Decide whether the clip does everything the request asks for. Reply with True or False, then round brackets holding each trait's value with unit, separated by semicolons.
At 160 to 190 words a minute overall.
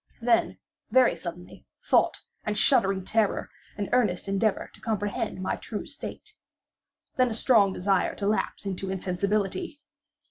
False (135 wpm)